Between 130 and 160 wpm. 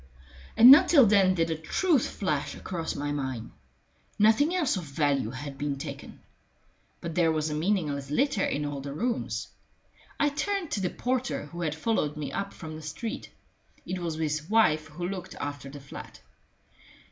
No: average, 175 wpm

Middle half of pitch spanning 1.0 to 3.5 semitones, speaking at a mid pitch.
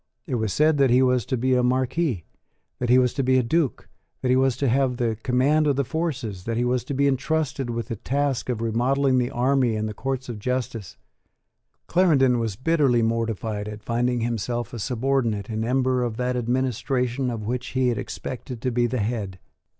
No: narrow, 2.4 semitones; low, 125 Hz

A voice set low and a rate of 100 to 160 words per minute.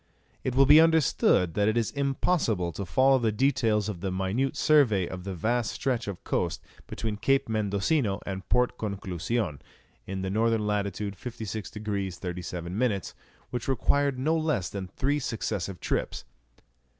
Yes: low, 110 Hz; average, 150 wpm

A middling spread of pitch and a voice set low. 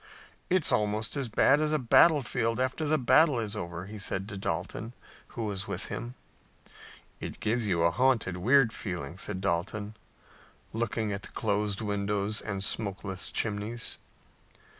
Yes: average, 3.5 semitones; low, 105 Hz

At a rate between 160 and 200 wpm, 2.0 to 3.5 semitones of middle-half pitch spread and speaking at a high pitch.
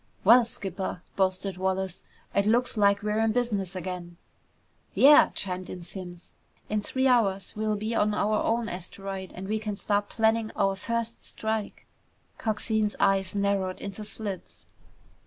No: average, 145 wpm; narrow, 2.5 semitones; high, 205 Hz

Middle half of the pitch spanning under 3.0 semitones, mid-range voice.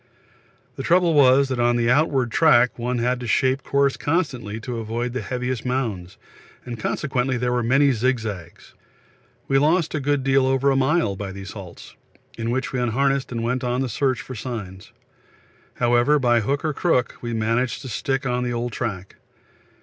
No: narrow, 2.6 semitones; low, 125 Hz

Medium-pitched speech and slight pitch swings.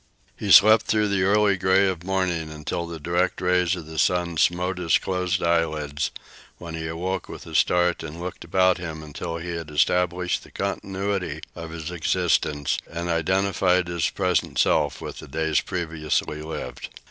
No: very low, 85 Hz; narrow, 2.3 semitones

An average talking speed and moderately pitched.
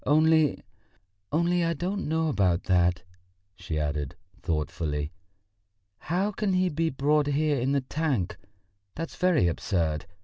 No: slow, 130 wpm; medium, 145 Hz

